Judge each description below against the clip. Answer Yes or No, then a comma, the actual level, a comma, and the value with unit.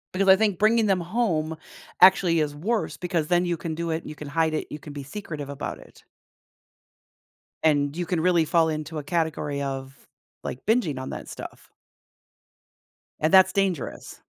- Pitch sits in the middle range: Yes, medium, 165 Hz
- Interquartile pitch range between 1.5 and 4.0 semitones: Yes, average, 3.6 semitones